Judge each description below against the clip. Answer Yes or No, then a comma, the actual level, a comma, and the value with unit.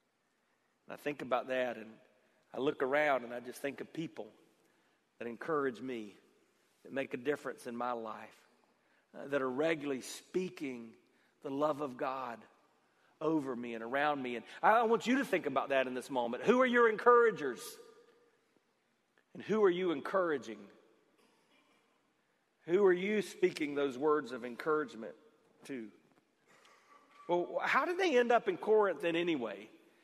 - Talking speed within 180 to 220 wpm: No, average, 150 wpm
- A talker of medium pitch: Yes, medium, 150 Hz